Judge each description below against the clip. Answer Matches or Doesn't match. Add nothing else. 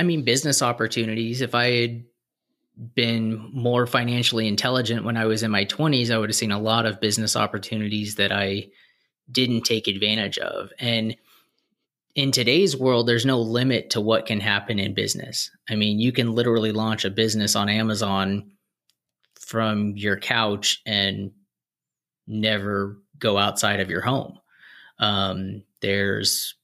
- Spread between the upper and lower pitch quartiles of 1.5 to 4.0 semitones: Matches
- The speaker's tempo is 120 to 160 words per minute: Matches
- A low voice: Matches